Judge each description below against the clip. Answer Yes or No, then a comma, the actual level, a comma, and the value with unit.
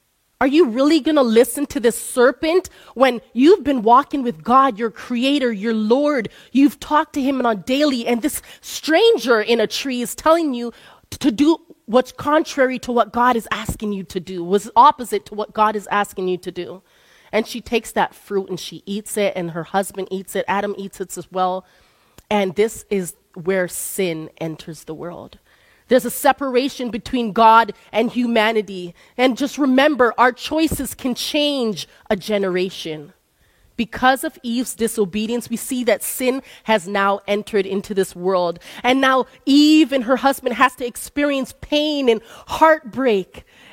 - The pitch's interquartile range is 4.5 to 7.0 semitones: Yes, average, 4.9 semitones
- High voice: Yes, high, 235 Hz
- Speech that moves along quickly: No, average, 170 wpm